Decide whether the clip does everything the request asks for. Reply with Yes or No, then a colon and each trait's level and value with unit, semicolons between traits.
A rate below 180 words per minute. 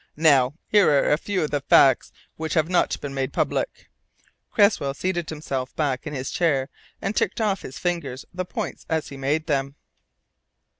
No: average, 185 wpm